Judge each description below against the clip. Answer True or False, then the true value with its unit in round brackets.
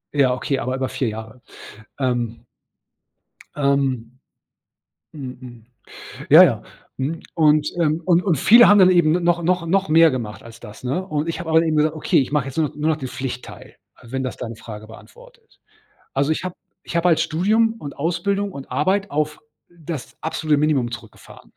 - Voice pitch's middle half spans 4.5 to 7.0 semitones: True (4.9 semitones)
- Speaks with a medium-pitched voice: True (150 Hz)